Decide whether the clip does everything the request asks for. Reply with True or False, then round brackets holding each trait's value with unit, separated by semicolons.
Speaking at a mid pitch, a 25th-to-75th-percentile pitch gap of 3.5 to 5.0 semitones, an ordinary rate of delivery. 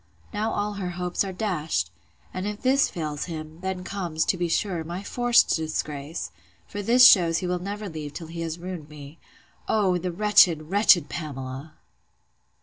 True (175 Hz; 4.2 semitones; 165 wpm)